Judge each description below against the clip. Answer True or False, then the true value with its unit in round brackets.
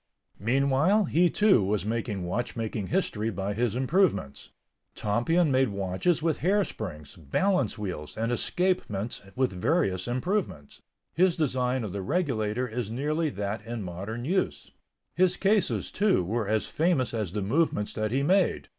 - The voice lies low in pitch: True (120 Hz)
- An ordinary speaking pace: True (145 wpm)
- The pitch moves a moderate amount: False (8.2 semitones)